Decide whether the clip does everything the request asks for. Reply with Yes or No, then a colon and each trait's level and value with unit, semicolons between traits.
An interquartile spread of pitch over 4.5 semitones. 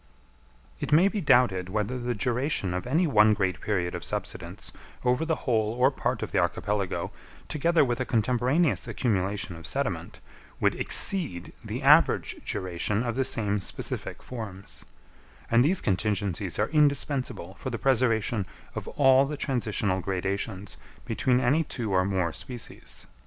Yes: average, 5.0 semitones